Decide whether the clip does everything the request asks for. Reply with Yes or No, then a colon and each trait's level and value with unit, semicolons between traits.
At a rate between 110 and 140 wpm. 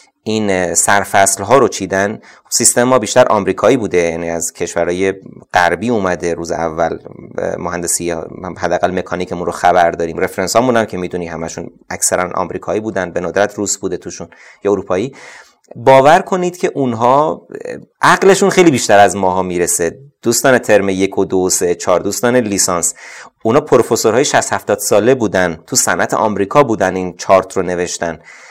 No: average, 150 wpm